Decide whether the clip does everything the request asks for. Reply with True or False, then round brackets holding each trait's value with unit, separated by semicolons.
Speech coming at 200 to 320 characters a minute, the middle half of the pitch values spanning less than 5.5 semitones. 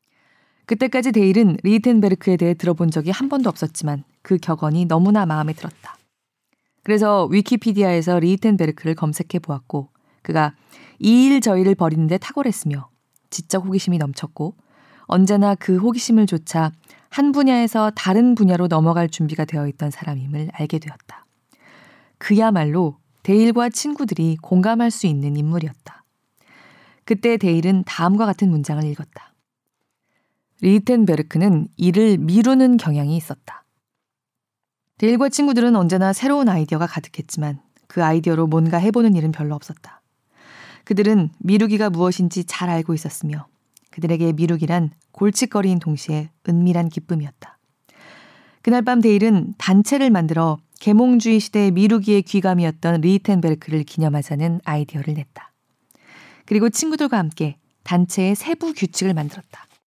False (335 characters per minute; 5.1 semitones)